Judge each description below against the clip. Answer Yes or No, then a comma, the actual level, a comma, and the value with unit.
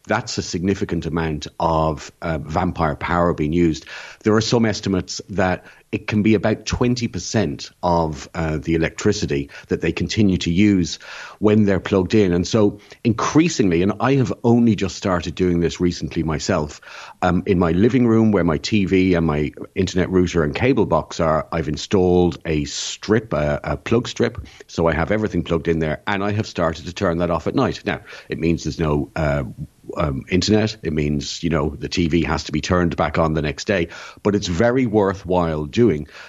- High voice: No, very low, 90 Hz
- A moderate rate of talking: Yes, average, 190 wpm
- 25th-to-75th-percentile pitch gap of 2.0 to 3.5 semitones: No, average, 4.1 semitones